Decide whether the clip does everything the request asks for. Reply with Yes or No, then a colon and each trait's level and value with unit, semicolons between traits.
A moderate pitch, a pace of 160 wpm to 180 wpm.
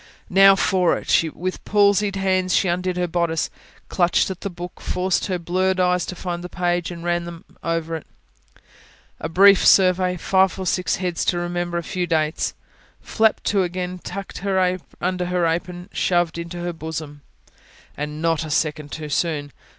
Yes: medium, 175 Hz; average, 170 wpm